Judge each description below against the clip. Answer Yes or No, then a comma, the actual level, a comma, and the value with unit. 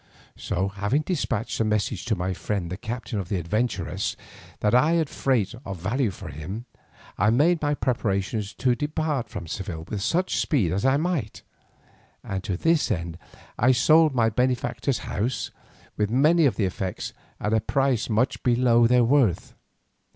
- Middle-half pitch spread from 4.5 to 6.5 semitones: Yes, wide, 5.4 semitones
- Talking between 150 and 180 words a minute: Yes, average, 165 wpm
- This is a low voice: Yes, low, 115 Hz